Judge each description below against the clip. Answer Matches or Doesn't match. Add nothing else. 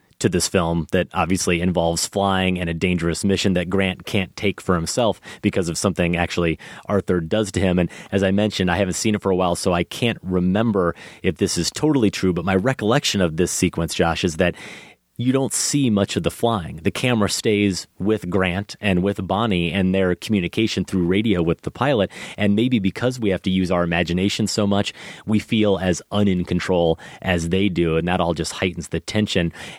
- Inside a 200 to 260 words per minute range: Matches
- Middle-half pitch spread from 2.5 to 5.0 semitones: Matches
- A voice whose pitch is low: Matches